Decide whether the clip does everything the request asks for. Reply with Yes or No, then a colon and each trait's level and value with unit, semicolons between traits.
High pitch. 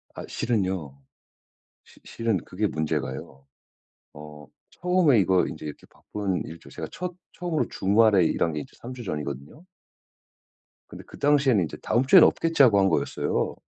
No: low, 100 Hz